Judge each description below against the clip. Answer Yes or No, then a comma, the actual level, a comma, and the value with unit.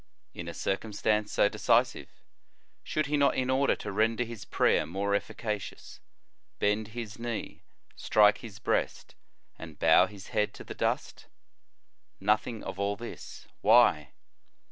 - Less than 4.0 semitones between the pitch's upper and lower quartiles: Yes, narrow, 2.6 semitones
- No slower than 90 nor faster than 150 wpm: Yes, average, 140 wpm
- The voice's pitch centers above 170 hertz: No, low, 105 Hz